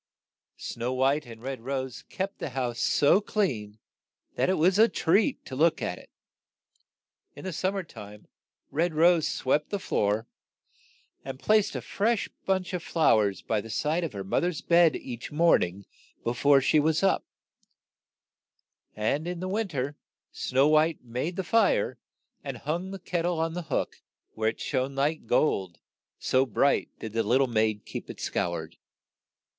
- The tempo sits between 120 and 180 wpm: Yes, average, 175 wpm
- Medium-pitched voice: Yes, medium, 145 Hz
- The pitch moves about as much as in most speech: No, wide, 7.0 semitones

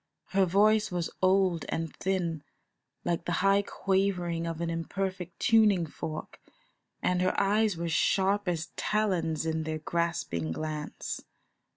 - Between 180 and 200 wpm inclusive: No, slow, 135 wpm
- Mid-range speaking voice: Yes, medium, 175 Hz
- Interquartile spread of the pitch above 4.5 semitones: No, average, 2.9 semitones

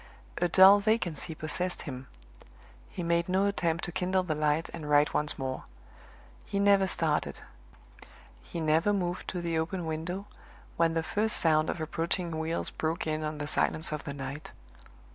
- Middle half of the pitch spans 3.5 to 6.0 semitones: No, average, 2.7 semitones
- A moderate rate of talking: Yes, average, 165 wpm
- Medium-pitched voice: Yes, medium, 165 Hz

